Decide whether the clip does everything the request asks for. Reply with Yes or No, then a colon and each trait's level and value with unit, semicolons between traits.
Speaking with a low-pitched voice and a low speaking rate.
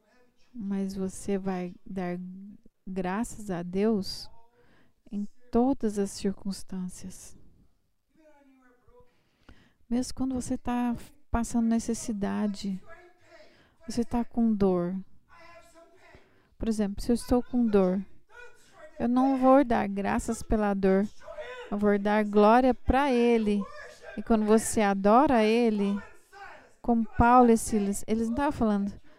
No: high, 230 Hz; slow, 110 wpm